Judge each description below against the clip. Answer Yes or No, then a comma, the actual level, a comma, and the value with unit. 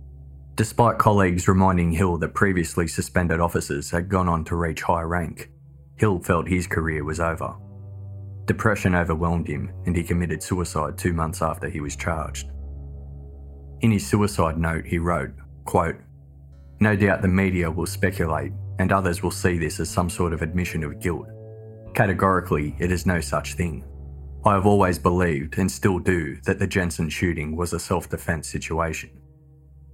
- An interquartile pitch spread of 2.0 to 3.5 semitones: No, average, 4.0 semitones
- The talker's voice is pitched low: Yes, very low, 85 Hz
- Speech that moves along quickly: No, average, 160 wpm